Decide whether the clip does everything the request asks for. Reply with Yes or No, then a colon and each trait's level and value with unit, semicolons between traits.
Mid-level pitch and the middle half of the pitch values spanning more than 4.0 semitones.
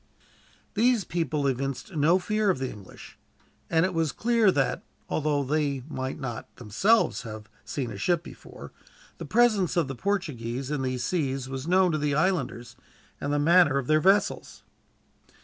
Yes: medium, 150 Hz; wide, 5.6 semitones